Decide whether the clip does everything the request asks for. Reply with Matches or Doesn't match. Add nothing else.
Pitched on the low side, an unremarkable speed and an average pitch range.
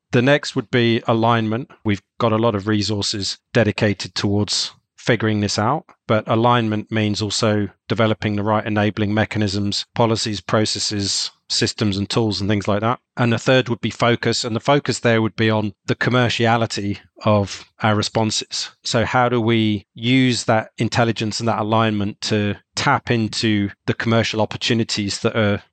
Doesn't match